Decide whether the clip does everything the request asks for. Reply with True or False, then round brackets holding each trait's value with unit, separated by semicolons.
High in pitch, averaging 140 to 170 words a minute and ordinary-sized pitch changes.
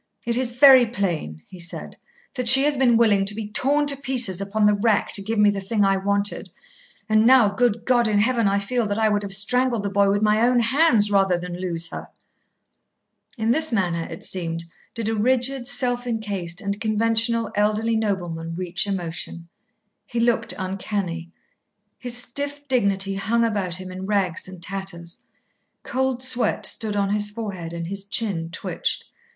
False (210 Hz; 180 wpm; 3.6 semitones)